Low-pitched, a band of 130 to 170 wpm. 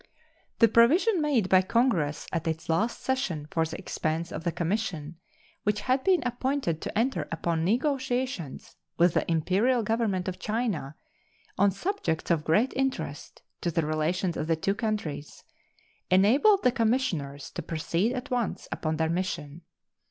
No: high, 190 Hz; average, 150 wpm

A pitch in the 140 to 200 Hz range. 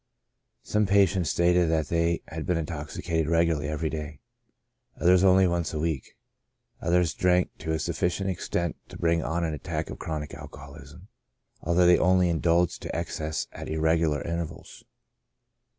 No: very low, 85 Hz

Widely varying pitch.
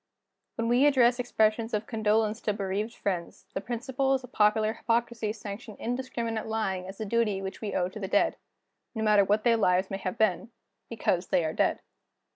No: average, 2.8 semitones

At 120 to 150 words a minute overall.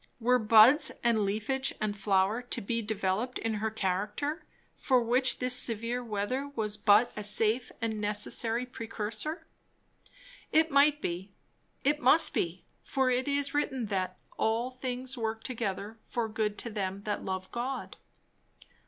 Yes: average, 145 wpm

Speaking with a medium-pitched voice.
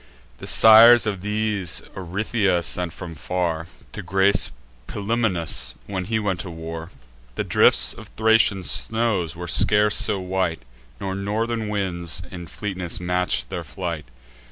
No: very low, 95 Hz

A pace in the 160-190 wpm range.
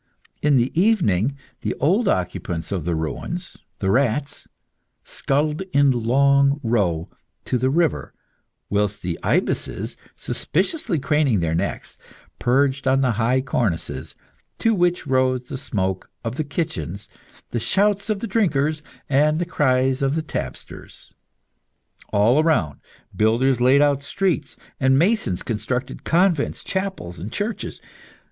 No: slow, 135 wpm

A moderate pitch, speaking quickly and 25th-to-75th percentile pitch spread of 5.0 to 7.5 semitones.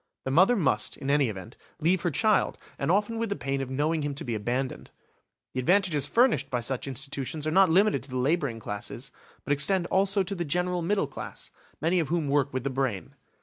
Yes: medium, 145 Hz; fast, 215 wpm; wide, 5.4 semitones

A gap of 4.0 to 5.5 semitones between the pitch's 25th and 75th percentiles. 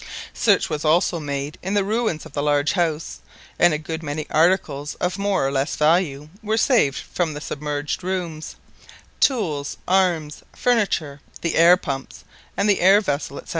Yes: average, 4.3 semitones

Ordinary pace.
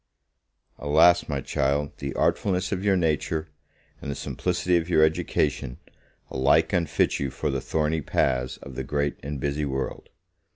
Yes: average, 155 wpm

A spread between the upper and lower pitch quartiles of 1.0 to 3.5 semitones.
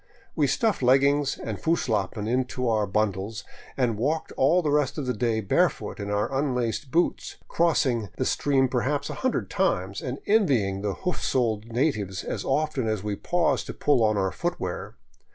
No: wide, 5.4 semitones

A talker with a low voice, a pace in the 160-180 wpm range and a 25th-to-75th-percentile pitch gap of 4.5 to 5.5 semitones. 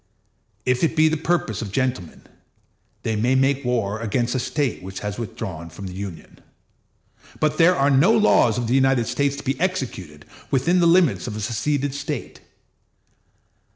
Yes: low, 130 Hz; average, 170 wpm; average, 5.2 semitones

